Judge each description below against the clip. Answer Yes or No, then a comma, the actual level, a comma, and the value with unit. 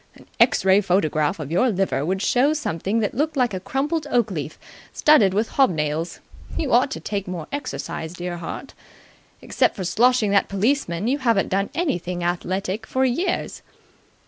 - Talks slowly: No, average, 170 wpm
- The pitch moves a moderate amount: No, wide, 6.4 semitones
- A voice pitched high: Yes, high, 200 Hz